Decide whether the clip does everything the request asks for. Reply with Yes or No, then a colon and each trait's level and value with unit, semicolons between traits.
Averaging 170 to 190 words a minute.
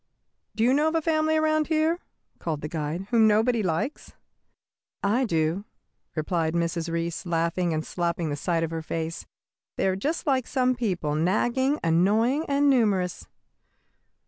No: average, 155 wpm